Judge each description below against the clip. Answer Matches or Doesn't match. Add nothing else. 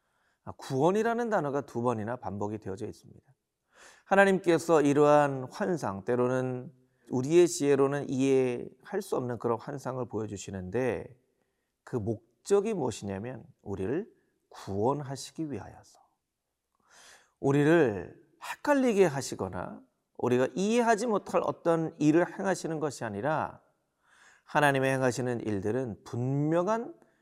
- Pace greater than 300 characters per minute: Doesn't match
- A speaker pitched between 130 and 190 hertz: Matches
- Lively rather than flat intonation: Matches